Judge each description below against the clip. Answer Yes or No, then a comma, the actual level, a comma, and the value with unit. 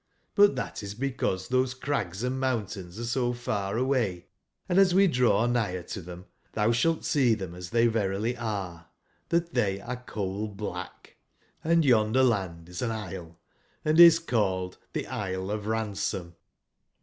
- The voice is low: Yes, low, 110 Hz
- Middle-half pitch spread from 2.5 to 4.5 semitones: No, average, 5.0 semitones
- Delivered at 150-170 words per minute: Yes, average, 155 wpm